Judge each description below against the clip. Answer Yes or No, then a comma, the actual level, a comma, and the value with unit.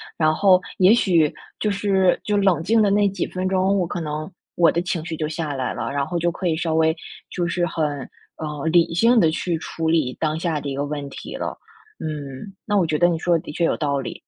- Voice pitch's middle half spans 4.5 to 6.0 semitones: No, average, 3.2 semitones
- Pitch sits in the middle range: Yes, medium, 165 Hz